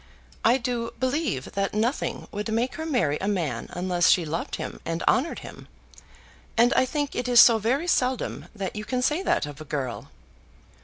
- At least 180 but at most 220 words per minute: Yes, average, 190 wpm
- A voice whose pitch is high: Yes, high, 230 Hz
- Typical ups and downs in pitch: No, wide, 6.5 semitones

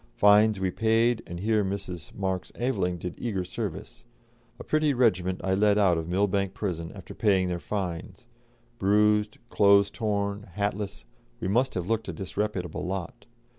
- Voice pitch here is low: Yes, low, 100 Hz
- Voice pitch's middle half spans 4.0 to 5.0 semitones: No, narrow, 2.4 semitones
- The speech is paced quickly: No, average, 155 wpm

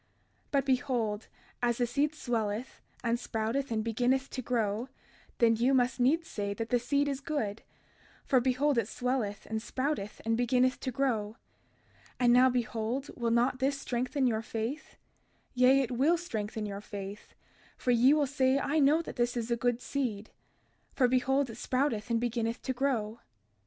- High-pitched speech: Yes, high, 245 Hz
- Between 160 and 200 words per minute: Yes, average, 170 wpm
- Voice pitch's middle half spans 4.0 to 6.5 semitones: No, average, 2.9 semitones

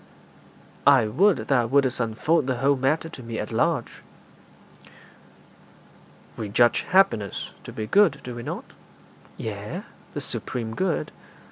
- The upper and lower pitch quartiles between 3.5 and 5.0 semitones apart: Yes, average, 4.3 semitones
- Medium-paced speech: No, slow, 130 wpm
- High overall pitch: No, low, 125 Hz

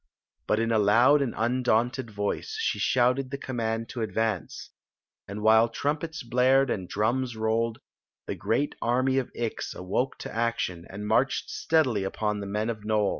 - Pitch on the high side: No, low, 115 Hz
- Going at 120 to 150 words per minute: No, average, 170 wpm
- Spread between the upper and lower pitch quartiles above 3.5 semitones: No, average, 3.2 semitones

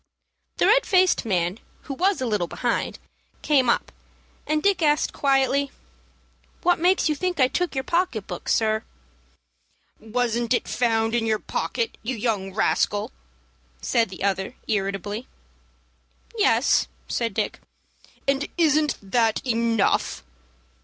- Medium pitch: No, high, 240 Hz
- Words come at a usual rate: No, slow, 130 wpm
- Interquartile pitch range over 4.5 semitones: Yes, wide, 5.5 semitones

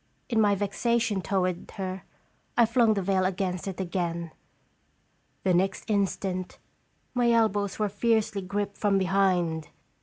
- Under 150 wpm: Yes, average, 140 wpm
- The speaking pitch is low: No, high, 195 Hz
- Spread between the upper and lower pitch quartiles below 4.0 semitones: Yes, narrow, 2.4 semitones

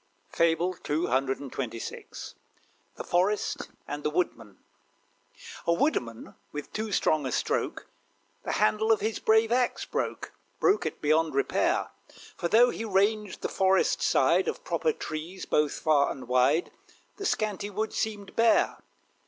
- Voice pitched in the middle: Yes, medium, 180 Hz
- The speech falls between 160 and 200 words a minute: No, slow, 135 wpm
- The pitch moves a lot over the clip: Yes, wide, 6.5 semitones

